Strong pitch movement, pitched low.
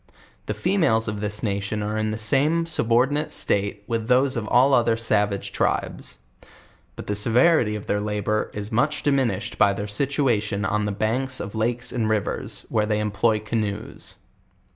No: average, 3.2 semitones; low, 110 Hz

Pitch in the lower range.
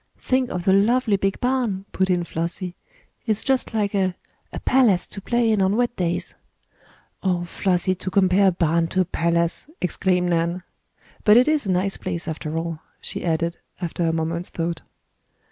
No: medium, 185 Hz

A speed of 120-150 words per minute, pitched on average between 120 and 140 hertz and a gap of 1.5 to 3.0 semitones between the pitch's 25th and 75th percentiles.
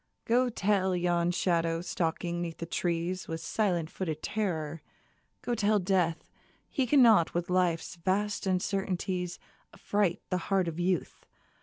No: slow, 135 wpm; medium, 180 Hz; average, 2.7 semitones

